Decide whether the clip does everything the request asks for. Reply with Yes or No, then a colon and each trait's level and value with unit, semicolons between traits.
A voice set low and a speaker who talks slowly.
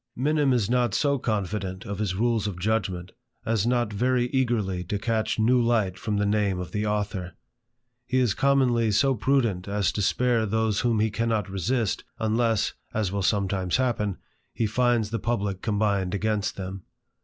No: low, 110 Hz; average, 170 wpm